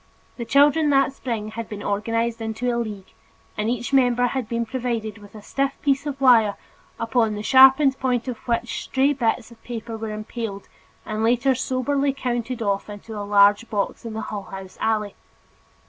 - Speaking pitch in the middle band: No, high, 230 Hz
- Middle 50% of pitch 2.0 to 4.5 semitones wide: Yes, average, 3.3 semitones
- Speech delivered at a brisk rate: No, average, 180 wpm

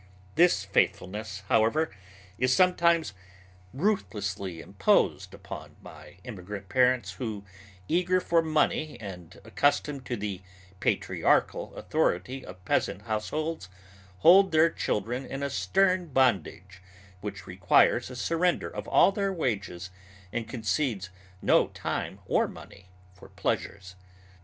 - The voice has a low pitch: Yes, low, 120 Hz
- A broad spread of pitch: Yes, wide, 8.3 semitones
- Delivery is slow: Yes, slow, 115 wpm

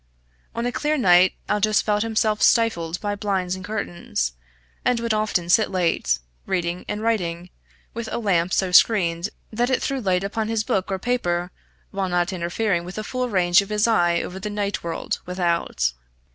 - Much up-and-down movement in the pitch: No, average, 3.7 semitones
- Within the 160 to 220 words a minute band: Yes, average, 180 wpm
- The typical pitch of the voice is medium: No, high, 195 Hz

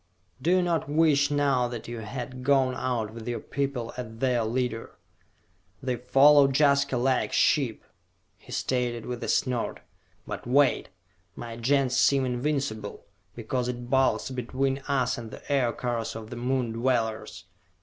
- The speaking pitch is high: No, low, 125 Hz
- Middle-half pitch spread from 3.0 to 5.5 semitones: No, narrow, 2.5 semitones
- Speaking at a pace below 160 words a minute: Yes, average, 150 wpm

